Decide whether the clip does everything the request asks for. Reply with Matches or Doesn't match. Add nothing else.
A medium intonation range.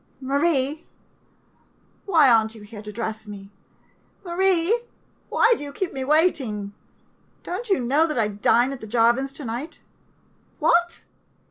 Doesn't match